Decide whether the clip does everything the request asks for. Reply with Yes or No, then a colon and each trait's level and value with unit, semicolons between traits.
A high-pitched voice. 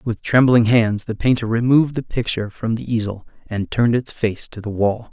No: low, 115 Hz